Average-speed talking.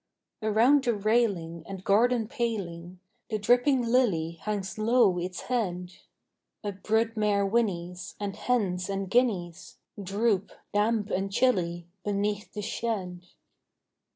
No: slow, 120 wpm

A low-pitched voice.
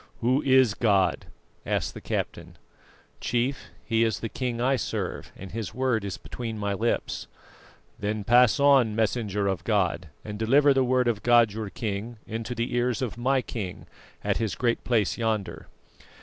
Yes: low, 115 Hz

